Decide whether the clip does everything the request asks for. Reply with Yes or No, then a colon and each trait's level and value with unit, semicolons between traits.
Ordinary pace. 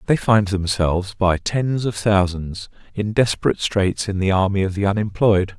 Yes: average, 170 wpm